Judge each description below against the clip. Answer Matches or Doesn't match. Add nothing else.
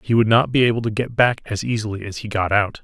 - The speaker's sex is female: Doesn't match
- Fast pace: Matches